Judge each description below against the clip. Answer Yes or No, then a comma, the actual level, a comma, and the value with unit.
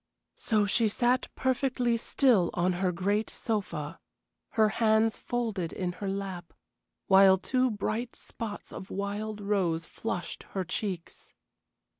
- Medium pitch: No, high, 205 Hz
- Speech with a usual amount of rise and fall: Yes, average, 3.3 semitones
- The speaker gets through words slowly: Yes, slow, 125 wpm